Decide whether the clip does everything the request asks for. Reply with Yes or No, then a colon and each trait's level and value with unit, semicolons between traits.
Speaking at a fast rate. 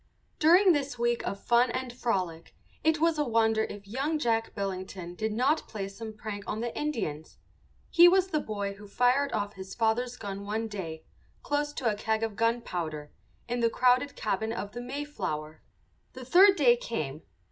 No: average, 180 wpm